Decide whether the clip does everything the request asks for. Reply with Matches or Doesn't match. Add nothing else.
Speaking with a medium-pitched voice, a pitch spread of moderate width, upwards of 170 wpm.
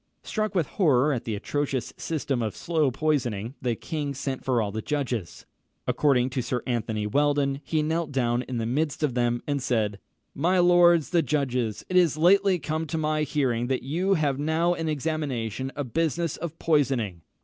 Matches